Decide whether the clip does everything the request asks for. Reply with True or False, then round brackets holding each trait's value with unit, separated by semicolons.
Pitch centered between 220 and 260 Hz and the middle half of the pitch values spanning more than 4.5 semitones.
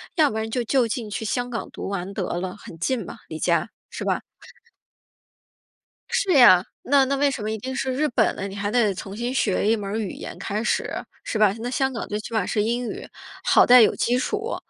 False (225 Hz; 3.8 semitones)